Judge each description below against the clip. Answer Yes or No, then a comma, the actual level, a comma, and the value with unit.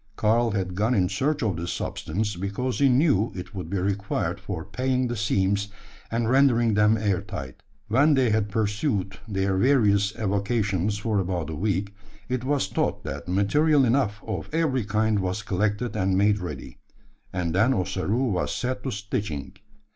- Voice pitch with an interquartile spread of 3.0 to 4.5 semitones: Yes, average, 4.0 semitones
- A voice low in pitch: Yes, low, 105 Hz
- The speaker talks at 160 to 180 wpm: Yes, average, 170 wpm